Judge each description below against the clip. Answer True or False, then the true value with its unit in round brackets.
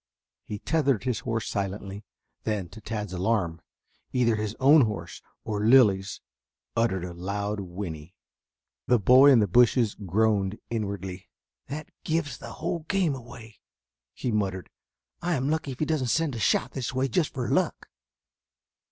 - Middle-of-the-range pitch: False (110 Hz)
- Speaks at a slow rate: False (150 wpm)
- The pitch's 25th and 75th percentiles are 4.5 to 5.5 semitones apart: True (4.9 semitones)